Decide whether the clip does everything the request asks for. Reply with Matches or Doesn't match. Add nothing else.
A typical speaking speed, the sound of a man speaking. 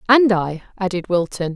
Doesn't match